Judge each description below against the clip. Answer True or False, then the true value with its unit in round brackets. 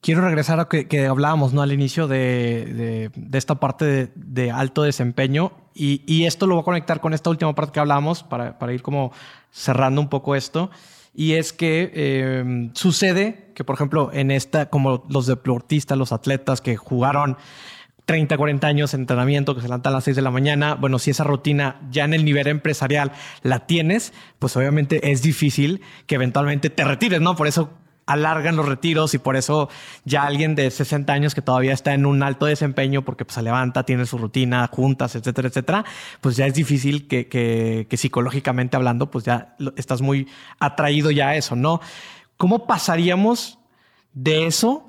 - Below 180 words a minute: False (190 wpm)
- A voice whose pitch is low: False (145 Hz)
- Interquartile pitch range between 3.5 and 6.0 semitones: False (3.0 semitones)